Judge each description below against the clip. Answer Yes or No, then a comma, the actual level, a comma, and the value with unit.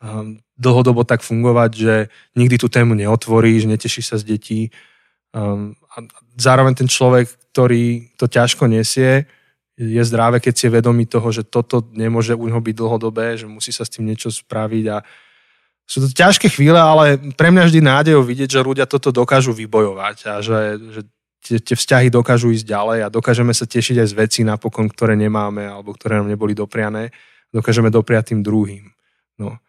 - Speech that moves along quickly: Yes, fast, 170 wpm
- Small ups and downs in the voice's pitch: Yes, narrow, 2.1 semitones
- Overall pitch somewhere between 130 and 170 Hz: No, low, 115 Hz